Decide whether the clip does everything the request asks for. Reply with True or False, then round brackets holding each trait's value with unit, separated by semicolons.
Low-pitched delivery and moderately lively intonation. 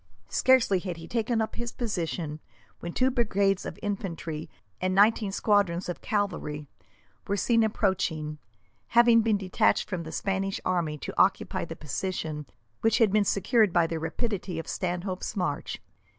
False (195 Hz; 4.3 semitones)